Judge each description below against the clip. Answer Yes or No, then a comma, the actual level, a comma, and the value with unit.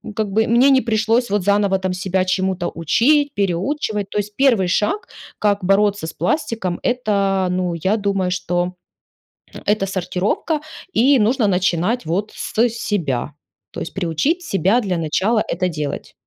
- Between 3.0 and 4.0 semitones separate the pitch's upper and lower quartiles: Yes, average, 3.6 semitones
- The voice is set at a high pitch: Yes, high, 200 Hz